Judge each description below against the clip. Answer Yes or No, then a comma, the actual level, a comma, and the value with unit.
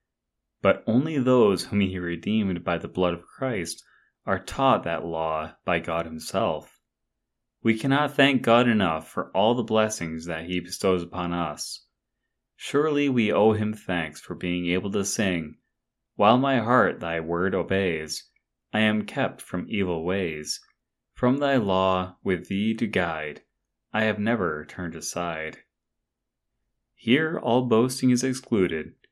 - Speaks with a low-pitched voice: Yes, very low, 95 Hz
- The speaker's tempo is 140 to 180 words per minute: Yes, average, 145 wpm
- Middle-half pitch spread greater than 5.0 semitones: Yes, wide, 5.4 semitones